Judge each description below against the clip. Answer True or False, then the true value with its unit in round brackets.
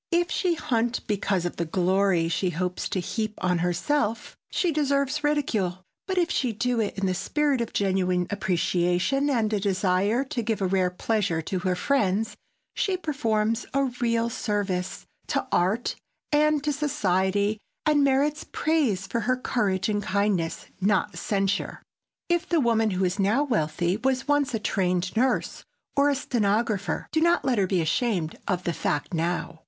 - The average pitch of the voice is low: False (210 Hz)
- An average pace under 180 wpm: True (165 wpm)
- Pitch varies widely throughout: True (6.4 semitones)